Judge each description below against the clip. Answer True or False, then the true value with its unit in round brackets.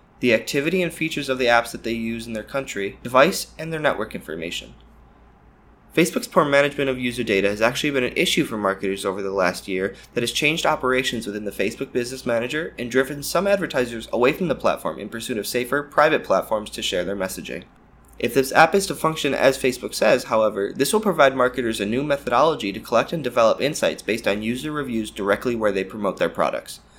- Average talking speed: False (210 wpm)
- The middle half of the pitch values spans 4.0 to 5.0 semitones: True (4.6 semitones)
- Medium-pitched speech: False (125 Hz)